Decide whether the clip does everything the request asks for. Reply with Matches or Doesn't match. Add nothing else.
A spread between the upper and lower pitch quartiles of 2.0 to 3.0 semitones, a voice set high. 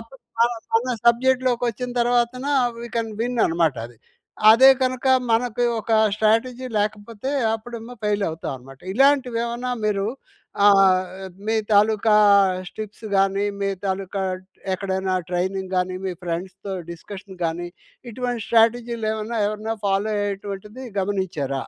Doesn't match